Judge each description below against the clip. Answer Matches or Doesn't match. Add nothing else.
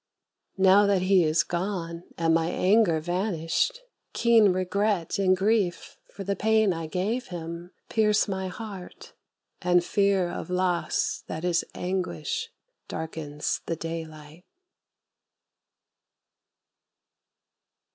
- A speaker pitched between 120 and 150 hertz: Doesn't match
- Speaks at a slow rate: Matches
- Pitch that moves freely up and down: Doesn't match